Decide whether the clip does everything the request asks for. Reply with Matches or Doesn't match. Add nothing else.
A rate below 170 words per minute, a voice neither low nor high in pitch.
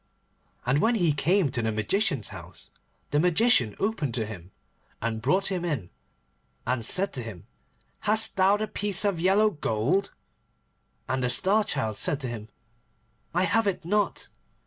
Matches